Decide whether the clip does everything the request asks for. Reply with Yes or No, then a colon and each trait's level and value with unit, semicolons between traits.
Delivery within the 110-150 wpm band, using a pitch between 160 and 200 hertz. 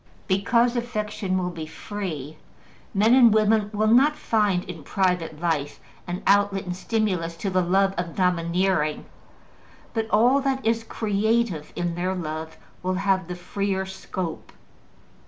Yes: average, 140 wpm; high, 190 Hz